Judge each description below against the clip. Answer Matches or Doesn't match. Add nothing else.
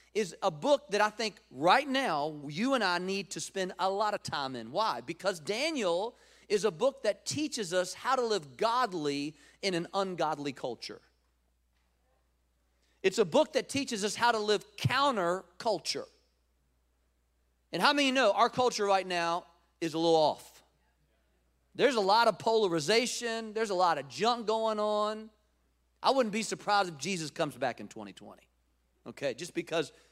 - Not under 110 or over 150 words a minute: Doesn't match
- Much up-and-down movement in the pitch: Matches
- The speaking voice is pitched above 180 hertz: Matches